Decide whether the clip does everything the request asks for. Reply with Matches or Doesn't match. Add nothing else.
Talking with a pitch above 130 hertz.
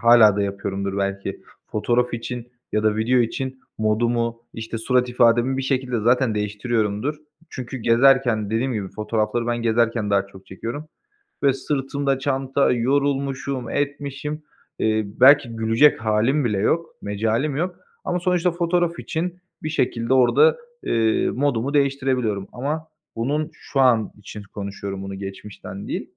Doesn't match